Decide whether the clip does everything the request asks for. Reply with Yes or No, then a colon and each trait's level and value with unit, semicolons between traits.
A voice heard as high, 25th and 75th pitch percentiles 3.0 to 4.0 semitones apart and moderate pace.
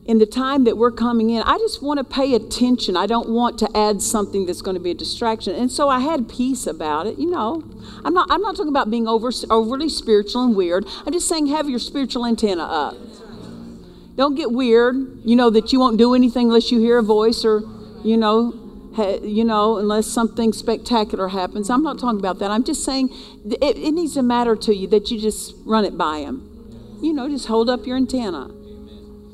No: high, 230 Hz; average, 3.3 semitones; fast, 220 wpm